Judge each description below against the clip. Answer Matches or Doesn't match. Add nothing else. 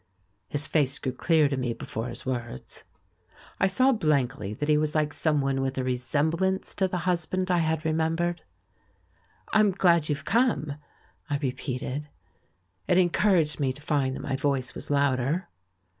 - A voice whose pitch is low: Doesn't match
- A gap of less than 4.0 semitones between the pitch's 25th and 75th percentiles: Doesn't match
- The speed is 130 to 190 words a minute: Matches